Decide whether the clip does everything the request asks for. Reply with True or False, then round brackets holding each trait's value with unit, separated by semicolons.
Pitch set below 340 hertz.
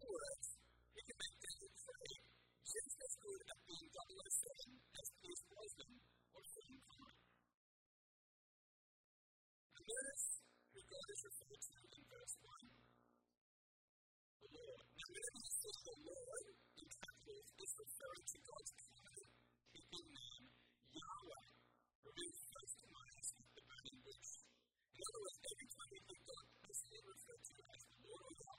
False (395 Hz)